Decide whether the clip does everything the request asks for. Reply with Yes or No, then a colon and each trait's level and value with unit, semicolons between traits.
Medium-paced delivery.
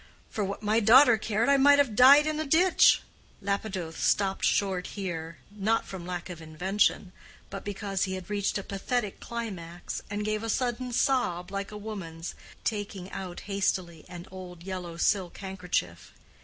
Yes: average, 165 wpm